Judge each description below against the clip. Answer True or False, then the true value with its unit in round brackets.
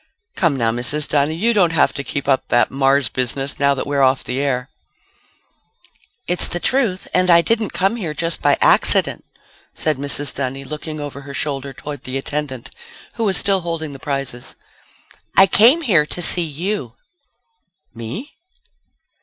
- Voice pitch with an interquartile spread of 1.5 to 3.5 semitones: False (4.5 semitones)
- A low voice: False (145 Hz)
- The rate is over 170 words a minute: False (165 wpm)